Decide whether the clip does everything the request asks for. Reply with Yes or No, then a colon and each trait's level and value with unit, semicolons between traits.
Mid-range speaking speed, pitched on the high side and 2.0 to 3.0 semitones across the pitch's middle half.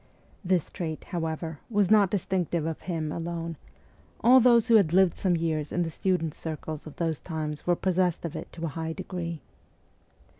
No: average, 180 wpm; medium, 170 Hz; average, 2.7 semitones